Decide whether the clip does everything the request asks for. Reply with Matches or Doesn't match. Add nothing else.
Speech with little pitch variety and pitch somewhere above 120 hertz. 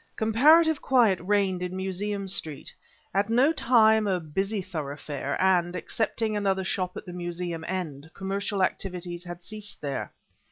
Doesn't match